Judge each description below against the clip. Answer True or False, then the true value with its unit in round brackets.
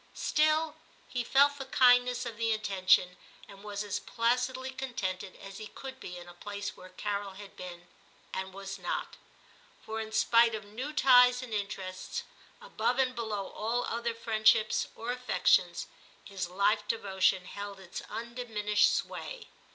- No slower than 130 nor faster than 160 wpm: True (155 wpm)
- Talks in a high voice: True (220 Hz)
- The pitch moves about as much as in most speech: True (4.0 semitones)